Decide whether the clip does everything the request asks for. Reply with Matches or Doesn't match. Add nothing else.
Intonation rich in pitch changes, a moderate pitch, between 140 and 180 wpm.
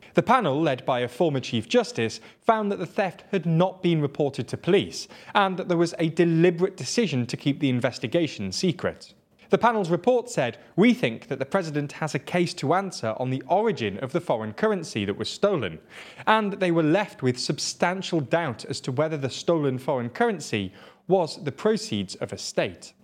Doesn't match